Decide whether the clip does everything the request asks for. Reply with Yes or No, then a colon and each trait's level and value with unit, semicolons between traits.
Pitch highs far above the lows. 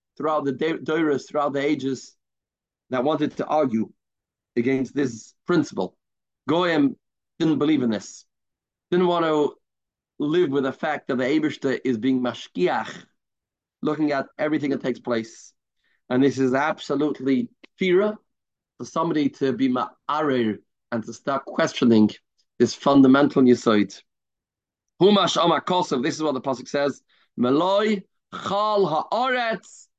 No: average, 3.9 semitones